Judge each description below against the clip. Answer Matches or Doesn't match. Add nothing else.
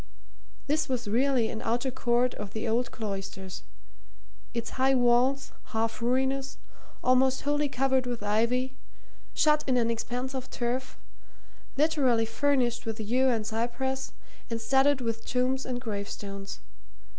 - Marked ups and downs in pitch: Doesn't match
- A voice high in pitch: Matches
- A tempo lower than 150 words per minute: Matches